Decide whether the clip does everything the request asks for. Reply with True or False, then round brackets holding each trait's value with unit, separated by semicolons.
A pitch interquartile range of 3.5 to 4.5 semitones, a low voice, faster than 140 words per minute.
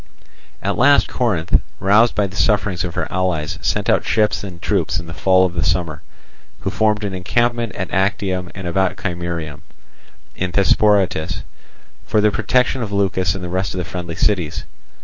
False (3.1 semitones; 95 Hz; 175 wpm)